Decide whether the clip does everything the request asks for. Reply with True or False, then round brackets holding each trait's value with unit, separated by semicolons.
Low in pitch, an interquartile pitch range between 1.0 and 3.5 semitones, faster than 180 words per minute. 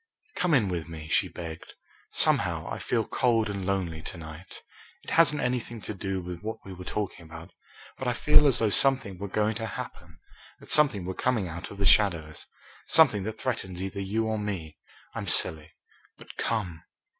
False (100 Hz; 4.5 semitones; 190 wpm)